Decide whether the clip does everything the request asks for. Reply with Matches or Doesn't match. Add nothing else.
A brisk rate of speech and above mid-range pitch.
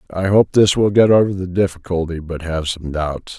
Doesn't match